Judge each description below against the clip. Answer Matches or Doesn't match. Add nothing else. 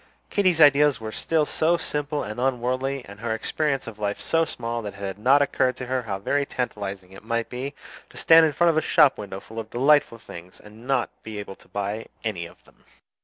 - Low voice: Matches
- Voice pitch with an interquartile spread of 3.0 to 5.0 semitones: Doesn't match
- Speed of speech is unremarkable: Doesn't match